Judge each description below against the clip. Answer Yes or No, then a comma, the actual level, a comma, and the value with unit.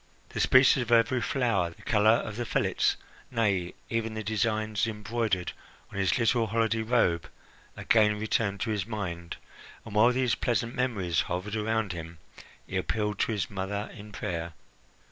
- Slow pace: No, average, 160 wpm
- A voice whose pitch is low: Yes, low, 110 Hz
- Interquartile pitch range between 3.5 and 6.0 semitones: No, average, 2.9 semitones